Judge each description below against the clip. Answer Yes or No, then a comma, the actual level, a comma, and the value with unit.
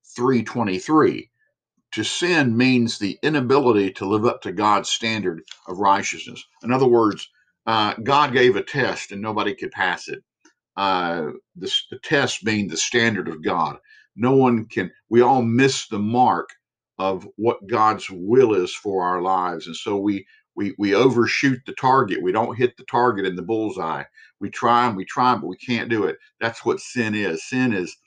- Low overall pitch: Yes, low, 115 Hz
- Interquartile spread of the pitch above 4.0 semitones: Yes, average, 4.9 semitones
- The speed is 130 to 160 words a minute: No, average, 180 wpm